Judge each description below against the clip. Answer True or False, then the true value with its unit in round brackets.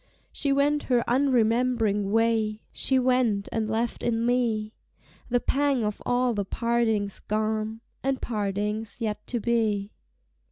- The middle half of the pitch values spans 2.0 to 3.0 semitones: True (2.6 semitones)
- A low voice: False (225 Hz)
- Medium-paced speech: False (130 wpm)